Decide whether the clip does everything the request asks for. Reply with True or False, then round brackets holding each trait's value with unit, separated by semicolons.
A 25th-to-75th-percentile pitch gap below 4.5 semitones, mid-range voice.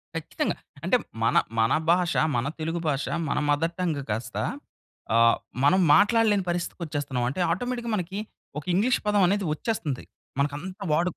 False (5.6 semitones; 175 Hz)